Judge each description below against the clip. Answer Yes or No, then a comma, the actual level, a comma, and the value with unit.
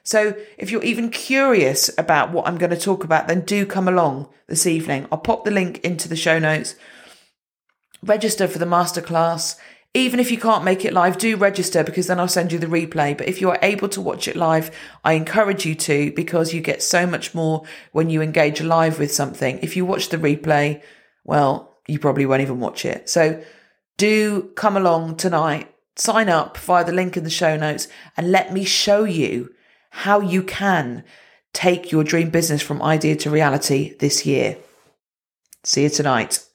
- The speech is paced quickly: No, average, 195 wpm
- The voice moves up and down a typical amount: Yes, average, 3.5 semitones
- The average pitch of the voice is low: No, medium, 170 Hz